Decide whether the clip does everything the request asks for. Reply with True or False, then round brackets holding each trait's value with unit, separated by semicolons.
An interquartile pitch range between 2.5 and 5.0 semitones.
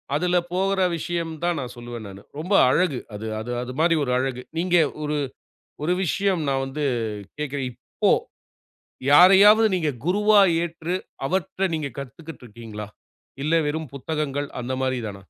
False (5.6 semitones)